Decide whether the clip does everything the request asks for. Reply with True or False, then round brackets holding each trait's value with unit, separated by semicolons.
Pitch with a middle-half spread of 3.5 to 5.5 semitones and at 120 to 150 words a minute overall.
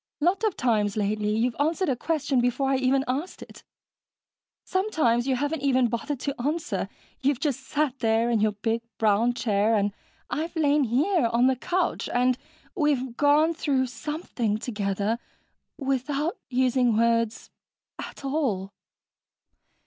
True (4.3 semitones; 140 wpm)